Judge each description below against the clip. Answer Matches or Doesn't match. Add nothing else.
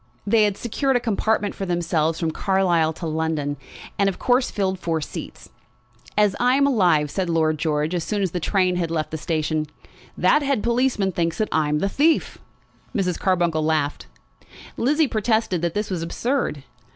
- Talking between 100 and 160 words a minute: Doesn't match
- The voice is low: Doesn't match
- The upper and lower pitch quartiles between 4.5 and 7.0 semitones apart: Matches